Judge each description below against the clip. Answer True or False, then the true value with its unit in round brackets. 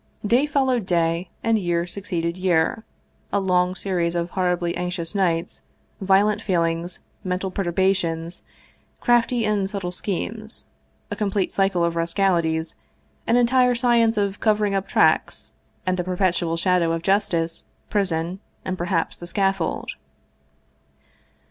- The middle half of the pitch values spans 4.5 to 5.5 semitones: False (3.1 semitones)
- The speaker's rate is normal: False (125 wpm)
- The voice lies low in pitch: False (185 Hz)